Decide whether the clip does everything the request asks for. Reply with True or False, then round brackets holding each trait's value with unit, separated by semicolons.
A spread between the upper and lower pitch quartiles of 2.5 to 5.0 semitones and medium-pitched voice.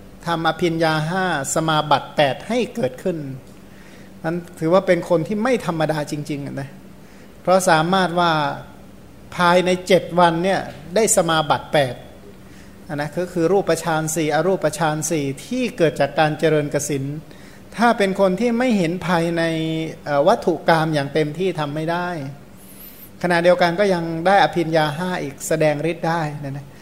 True (3.0 semitones; 165 Hz)